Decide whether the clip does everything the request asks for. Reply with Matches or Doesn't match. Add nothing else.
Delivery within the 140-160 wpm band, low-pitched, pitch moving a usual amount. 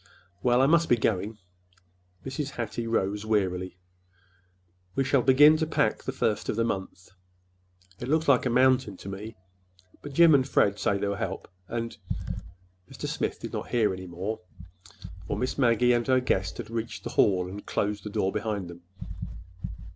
Doesn't match